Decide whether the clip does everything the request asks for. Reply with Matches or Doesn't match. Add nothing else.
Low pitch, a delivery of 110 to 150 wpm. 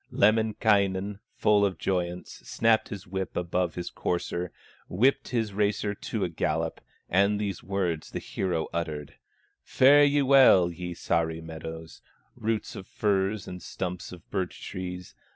Matches